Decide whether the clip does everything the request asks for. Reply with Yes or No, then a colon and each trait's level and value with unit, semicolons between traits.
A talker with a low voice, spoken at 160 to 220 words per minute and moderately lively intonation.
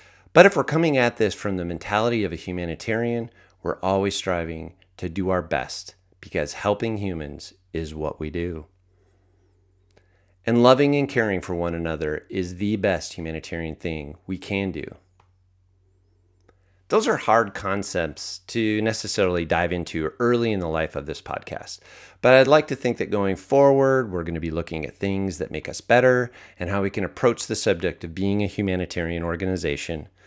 Yes: very low, 95 Hz; average, 170 wpm; average, 3.7 semitones